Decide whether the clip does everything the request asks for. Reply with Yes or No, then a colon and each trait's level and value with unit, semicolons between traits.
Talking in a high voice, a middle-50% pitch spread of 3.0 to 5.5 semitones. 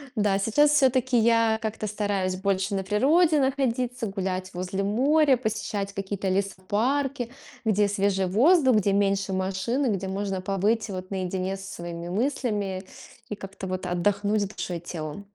Yes: high, 200 Hz; average, 3.5 semitones